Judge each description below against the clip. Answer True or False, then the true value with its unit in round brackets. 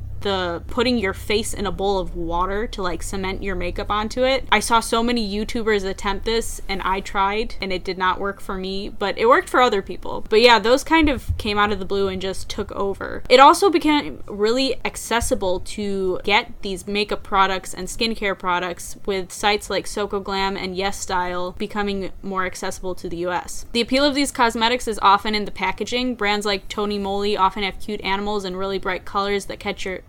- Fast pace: True (210 wpm)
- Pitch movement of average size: True (3.0 semitones)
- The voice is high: True (200 Hz)